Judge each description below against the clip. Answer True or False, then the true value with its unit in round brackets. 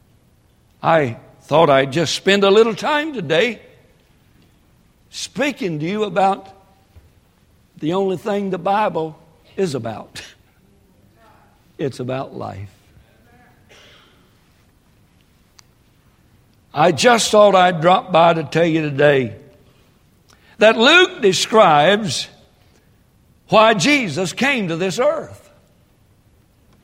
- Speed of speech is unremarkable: False (95 wpm)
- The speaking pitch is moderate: True (180 Hz)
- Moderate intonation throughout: False (7.4 semitones)